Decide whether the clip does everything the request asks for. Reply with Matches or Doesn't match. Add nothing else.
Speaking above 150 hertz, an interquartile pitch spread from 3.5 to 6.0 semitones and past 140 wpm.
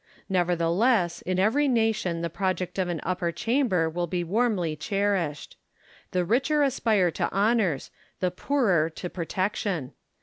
Doesn't match